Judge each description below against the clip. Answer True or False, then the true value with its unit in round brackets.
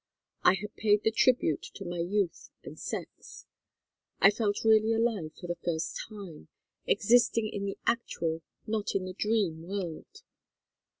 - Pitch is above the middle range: True (205 Hz)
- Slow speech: False (145 wpm)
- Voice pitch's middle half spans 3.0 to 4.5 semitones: True (4.1 semitones)